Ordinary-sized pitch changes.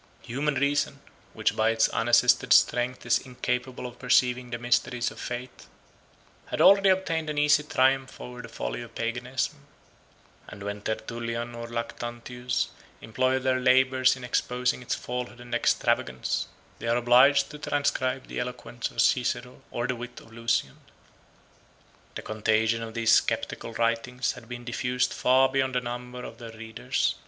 No: narrow, 1.7 semitones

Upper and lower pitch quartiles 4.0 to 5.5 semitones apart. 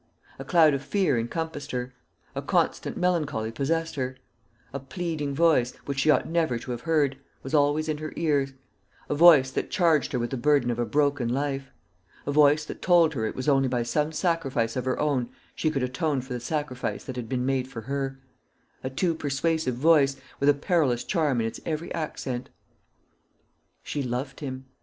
No: average, 3.4 semitones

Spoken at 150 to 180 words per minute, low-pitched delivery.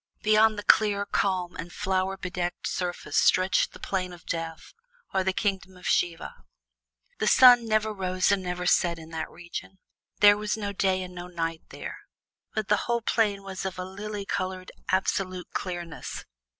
No: average, 170 wpm; medium, 185 Hz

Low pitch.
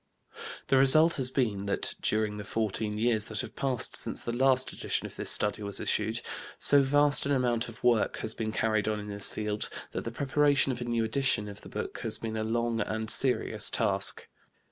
Yes: low, 115 Hz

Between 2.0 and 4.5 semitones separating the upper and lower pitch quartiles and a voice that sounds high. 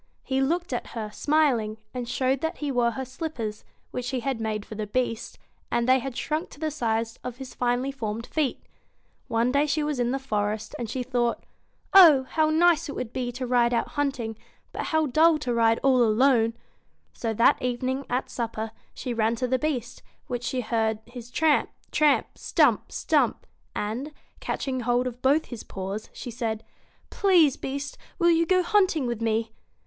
Yes: average, 3.7 semitones; very high, 250 Hz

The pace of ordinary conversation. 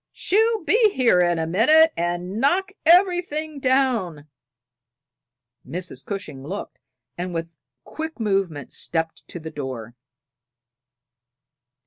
No: slow, 115 wpm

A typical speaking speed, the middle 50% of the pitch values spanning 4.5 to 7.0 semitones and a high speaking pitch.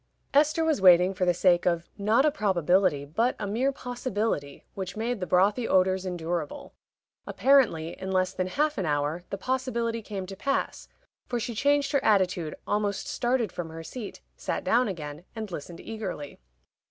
Yes: average, 170 wpm; wide, 5.5 semitones; high, 195 Hz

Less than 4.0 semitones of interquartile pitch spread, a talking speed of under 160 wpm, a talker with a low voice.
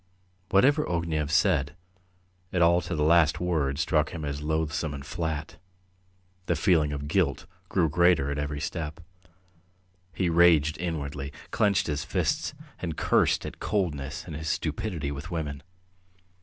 Yes: average, 2.9 semitones; average, 140 wpm; very low, 80 Hz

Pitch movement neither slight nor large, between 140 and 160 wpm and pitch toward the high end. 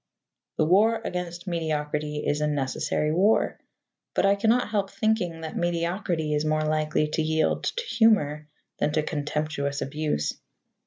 No: average, 3.5 semitones; average, 145 wpm; medium, 155 Hz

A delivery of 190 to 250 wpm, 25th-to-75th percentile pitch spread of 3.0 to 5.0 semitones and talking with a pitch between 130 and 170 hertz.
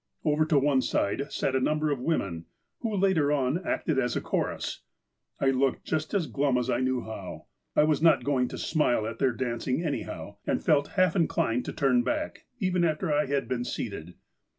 Yes: average, 195 wpm; average, 3.9 semitones; medium, 140 Hz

